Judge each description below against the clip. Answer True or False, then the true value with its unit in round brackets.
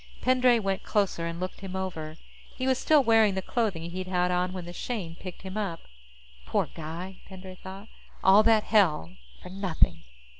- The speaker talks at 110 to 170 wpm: False (180 wpm)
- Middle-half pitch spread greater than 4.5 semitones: False (3.1 semitones)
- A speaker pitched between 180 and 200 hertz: True (190 Hz)